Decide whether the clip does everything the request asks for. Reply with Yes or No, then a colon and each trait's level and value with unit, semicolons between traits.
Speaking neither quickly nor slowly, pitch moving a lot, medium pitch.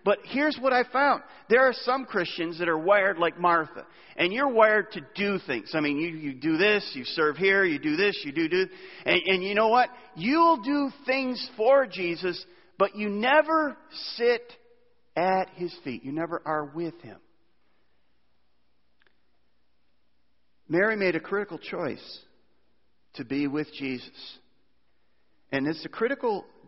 No: average, 160 wpm; wide, 8.4 semitones; high, 195 Hz